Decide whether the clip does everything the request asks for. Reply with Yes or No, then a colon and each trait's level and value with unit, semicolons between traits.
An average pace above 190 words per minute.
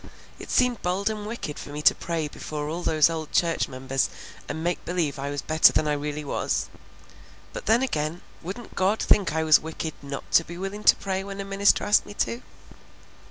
Yes: fast, 205 wpm